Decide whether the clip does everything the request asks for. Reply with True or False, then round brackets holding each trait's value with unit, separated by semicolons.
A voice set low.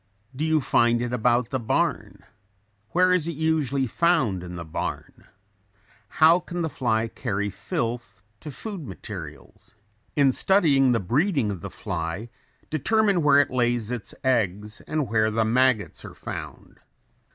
True (125 Hz)